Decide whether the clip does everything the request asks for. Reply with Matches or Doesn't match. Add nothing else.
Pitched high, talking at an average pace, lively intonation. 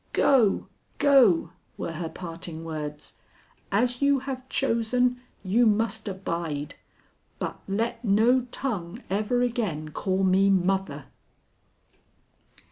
Doesn't match